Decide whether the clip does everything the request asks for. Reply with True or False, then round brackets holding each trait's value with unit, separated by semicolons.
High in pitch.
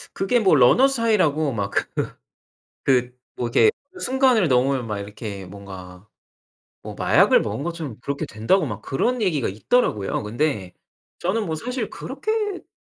False (140 Hz)